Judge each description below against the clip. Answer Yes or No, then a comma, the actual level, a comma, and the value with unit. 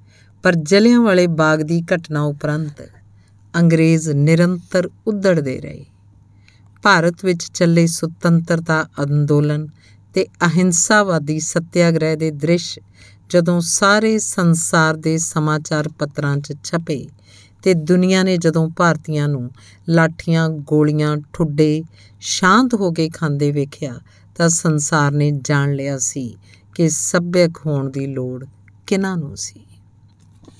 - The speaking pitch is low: No, medium, 155 Hz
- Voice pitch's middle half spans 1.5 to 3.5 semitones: No, average, 4.0 semitones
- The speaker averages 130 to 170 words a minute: No, average, 110 wpm